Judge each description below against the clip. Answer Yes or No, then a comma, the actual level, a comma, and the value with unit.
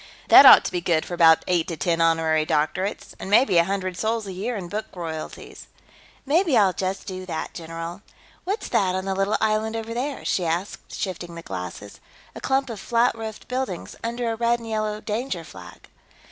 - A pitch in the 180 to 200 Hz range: Yes, high, 190 Hz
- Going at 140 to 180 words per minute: No, average, 200 wpm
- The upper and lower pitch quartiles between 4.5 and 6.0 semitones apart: Yes, average, 5.1 semitones